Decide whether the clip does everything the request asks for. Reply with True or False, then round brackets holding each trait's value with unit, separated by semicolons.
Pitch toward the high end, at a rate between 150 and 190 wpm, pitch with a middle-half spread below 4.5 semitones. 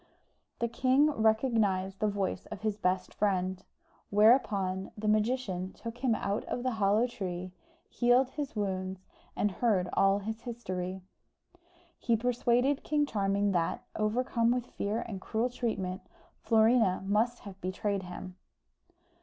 False (215 Hz; 135 wpm; 3.9 semitones)